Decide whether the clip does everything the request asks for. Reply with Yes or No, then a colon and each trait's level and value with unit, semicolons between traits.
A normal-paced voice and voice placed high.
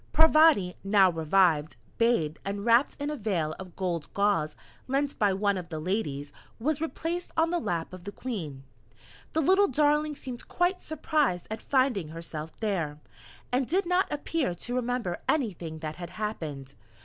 Yes: average, 160 wpm; high, 205 Hz